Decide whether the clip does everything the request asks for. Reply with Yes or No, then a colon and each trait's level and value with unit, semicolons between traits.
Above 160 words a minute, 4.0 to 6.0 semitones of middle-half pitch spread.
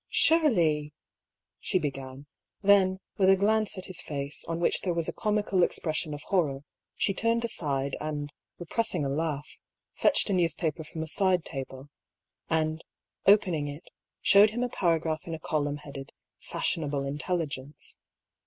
No: average, 155 wpm; average, 4.5 semitones